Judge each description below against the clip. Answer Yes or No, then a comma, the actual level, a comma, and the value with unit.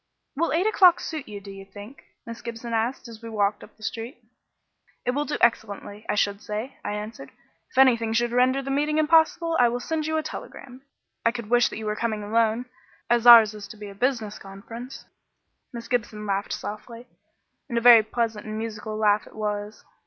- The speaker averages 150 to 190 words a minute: No, fast, 205 wpm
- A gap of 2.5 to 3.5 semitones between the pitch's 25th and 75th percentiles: Yes, average, 2.9 semitones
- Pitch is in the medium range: No, high, 230 Hz